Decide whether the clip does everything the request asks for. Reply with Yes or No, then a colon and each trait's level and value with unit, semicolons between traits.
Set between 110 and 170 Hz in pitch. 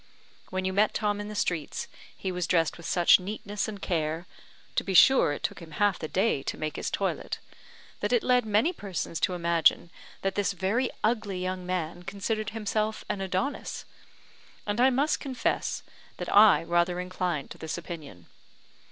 No: high, 190 Hz